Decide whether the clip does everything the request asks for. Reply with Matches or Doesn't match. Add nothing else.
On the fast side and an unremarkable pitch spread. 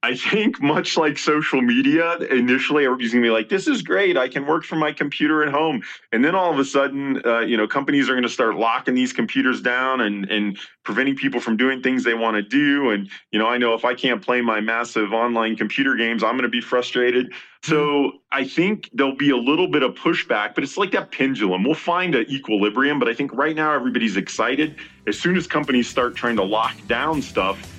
Matches